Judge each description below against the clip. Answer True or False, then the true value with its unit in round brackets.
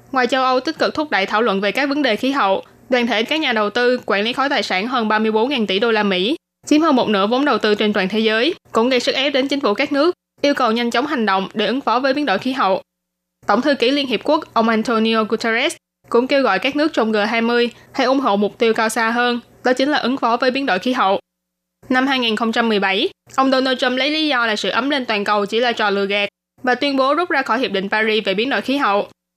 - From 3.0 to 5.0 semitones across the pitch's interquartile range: True (4.2 semitones)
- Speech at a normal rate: False (270 wpm)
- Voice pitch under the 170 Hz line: False (235 Hz)